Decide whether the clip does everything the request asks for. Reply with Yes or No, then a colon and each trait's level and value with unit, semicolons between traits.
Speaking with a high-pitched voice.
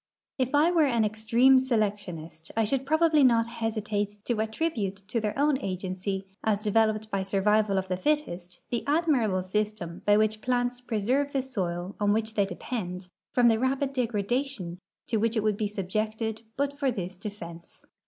Yes: high, 215 Hz